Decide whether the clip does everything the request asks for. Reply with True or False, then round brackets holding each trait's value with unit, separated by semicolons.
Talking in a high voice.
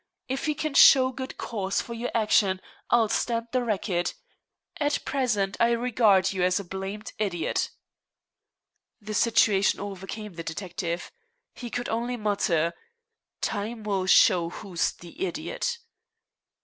True (210 Hz)